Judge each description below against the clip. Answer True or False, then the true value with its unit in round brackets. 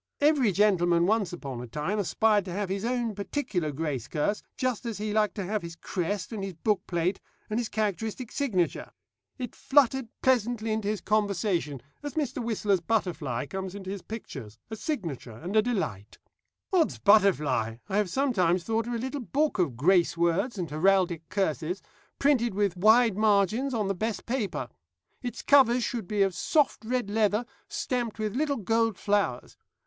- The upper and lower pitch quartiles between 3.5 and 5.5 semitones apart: True (4.6 semitones)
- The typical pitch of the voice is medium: False (205 Hz)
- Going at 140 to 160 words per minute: False (175 wpm)